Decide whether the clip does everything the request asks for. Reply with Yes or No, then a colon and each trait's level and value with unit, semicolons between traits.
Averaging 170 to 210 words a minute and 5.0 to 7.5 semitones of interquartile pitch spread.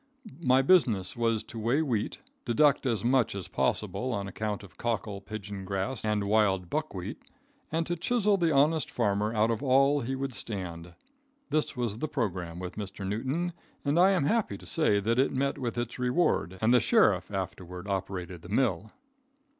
Yes: average, 180 wpm; wide, 5.6 semitones